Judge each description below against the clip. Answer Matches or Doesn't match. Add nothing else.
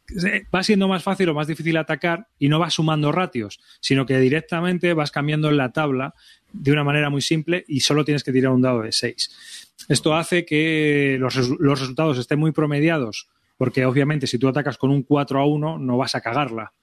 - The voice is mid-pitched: Matches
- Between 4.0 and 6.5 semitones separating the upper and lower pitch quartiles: Doesn't match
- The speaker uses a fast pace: Matches